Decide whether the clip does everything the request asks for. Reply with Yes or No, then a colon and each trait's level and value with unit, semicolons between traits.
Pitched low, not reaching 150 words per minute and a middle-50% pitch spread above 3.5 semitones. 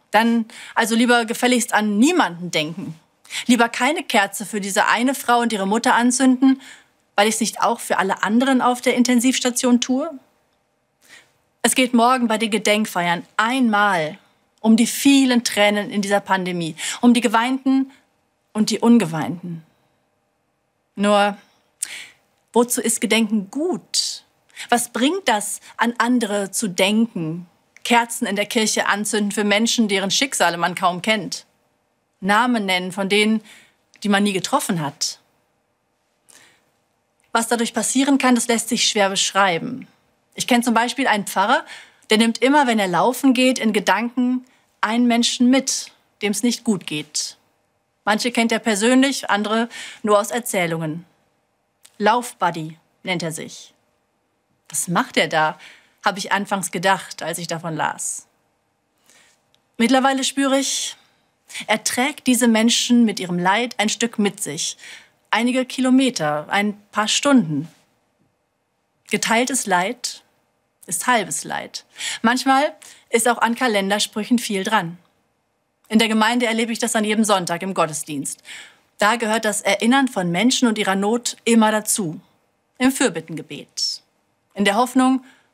No: high, 220 Hz; average, 140 wpm; average, 3.9 semitones